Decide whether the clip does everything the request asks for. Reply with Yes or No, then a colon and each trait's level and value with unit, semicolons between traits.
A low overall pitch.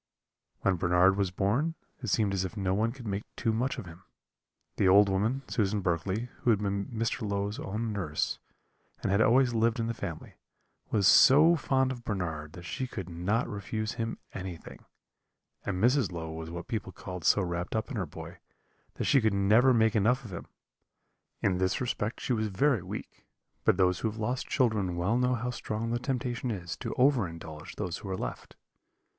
Yes: low, 105 Hz